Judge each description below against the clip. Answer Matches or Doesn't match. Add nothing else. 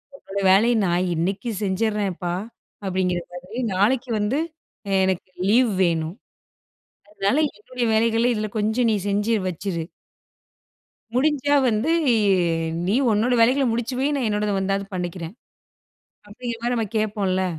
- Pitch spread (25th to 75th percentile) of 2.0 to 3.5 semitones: Doesn't match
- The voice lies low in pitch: Doesn't match